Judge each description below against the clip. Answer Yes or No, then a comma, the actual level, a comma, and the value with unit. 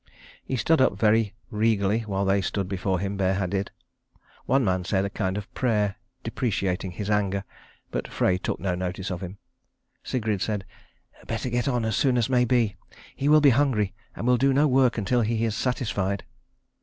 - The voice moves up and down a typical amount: Yes, average, 4.1 semitones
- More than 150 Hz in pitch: No, low, 105 Hz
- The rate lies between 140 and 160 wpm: No, average, 185 wpm